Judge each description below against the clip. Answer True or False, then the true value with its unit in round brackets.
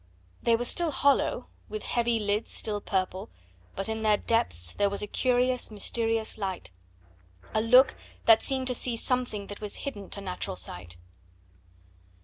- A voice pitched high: True (220 Hz)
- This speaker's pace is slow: False (155 wpm)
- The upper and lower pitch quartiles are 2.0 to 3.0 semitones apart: False (3.5 semitones)